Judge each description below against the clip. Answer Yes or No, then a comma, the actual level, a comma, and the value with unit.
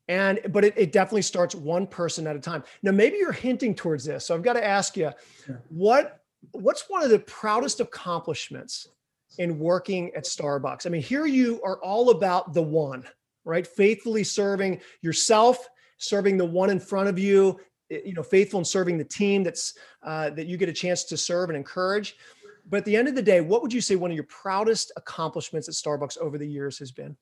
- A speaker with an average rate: No, fast, 210 wpm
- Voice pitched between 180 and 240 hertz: Yes, high, 190 Hz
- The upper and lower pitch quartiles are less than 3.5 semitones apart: No, average, 4.2 semitones